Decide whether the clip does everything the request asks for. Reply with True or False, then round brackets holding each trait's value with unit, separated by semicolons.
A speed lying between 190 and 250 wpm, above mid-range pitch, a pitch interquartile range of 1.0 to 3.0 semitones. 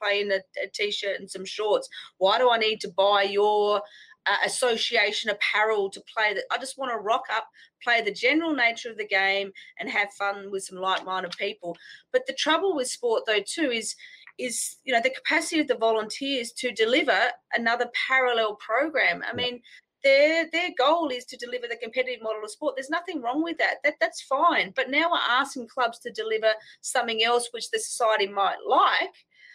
False (195 wpm; 235 Hz; 4.7 semitones)